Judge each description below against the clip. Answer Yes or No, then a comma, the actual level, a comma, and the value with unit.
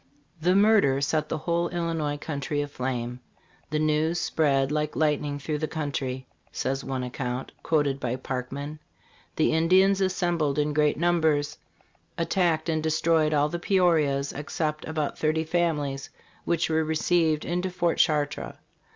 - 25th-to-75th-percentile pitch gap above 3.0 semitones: No, average, 2.7 semitones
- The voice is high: No, medium, 155 Hz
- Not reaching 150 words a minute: Yes, slow, 135 wpm